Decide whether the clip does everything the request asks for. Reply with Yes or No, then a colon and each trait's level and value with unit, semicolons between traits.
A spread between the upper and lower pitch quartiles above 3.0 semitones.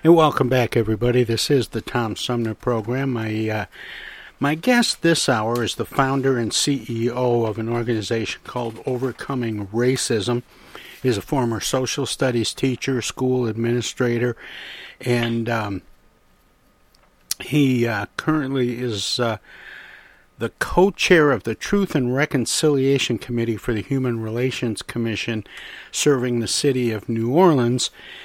No: average, 2.7 semitones